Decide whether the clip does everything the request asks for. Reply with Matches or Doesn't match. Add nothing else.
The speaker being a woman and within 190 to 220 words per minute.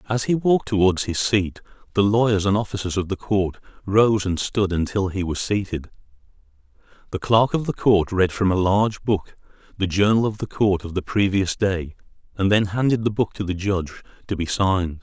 Doesn't match